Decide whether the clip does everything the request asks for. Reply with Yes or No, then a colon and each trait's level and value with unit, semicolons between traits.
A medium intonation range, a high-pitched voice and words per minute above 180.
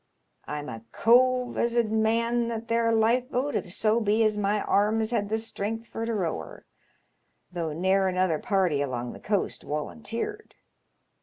No: average, 3.8 semitones; high, 220 Hz; average, 160 wpm